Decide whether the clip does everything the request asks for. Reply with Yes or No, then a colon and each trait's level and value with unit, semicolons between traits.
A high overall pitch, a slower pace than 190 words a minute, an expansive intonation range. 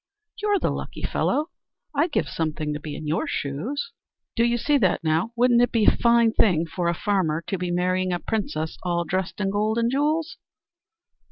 No: high, 195 Hz; average, 195 wpm; wide, 6.0 semitones